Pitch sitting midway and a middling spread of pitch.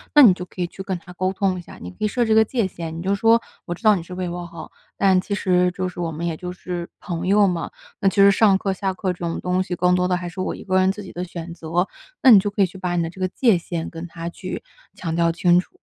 No: medium, 180 Hz; narrow, 1.9 semitones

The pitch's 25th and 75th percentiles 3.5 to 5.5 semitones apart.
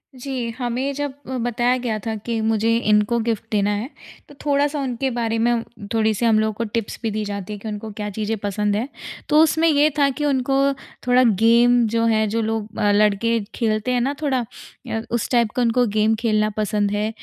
No: narrow, 2.6 semitones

